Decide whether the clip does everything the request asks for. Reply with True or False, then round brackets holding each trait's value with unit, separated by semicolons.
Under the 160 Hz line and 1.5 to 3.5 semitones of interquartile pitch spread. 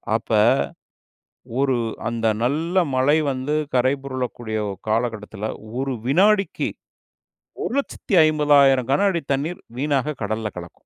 False (135 Hz; 4.2 semitones)